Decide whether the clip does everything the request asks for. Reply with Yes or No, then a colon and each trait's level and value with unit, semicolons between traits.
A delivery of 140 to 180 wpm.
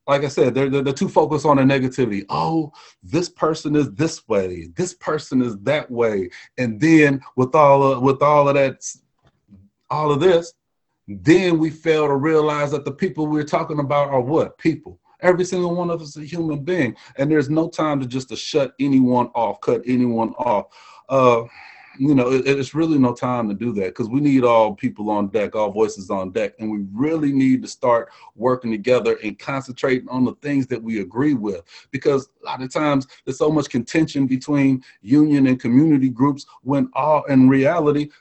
No: average, 200 wpm